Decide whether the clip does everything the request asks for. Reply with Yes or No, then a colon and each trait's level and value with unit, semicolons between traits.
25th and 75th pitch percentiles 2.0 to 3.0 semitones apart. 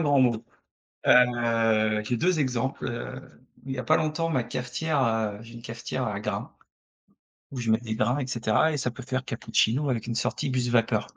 Yes: narrow, 2.6 semitones